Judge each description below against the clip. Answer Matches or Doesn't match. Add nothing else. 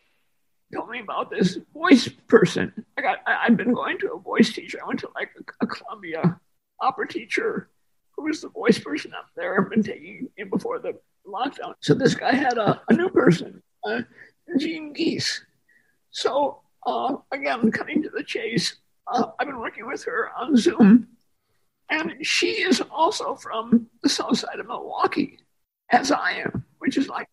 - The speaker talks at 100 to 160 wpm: Doesn't match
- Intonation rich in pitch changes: Matches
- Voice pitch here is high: Matches